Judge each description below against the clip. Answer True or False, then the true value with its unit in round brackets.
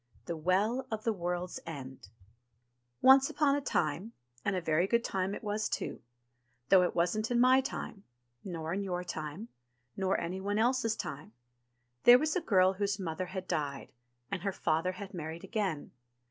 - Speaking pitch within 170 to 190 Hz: True (185 Hz)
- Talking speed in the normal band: True (165 wpm)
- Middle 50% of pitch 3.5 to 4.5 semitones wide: False (5.0 semitones)